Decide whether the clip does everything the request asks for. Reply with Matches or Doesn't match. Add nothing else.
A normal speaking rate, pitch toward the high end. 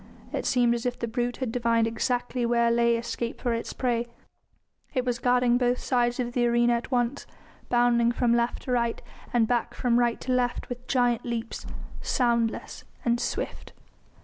Matches